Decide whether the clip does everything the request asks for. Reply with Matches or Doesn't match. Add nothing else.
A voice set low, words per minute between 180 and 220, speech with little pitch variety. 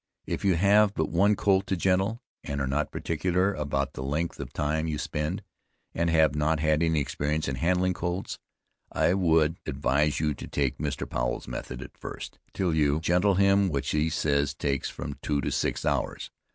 Doesn't match